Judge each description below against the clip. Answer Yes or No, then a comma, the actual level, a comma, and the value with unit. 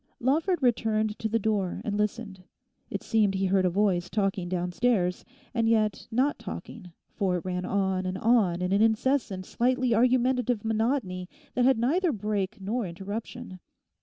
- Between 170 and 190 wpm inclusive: No, average, 160 wpm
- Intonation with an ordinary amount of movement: Yes, average, 4.2 semitones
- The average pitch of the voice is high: Yes, high, 215 Hz